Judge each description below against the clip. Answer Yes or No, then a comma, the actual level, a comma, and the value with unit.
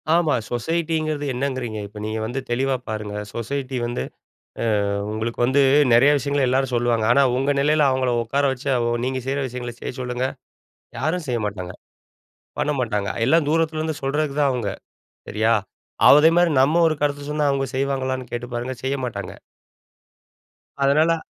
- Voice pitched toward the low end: Yes, low, 130 Hz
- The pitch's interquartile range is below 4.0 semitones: Yes, average, 3.5 semitones